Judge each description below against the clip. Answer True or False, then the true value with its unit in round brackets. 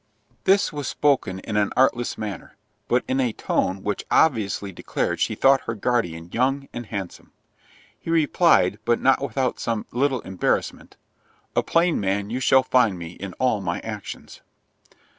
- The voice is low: True (115 Hz)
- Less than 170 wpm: True (160 wpm)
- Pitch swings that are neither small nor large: True (5.0 semitones)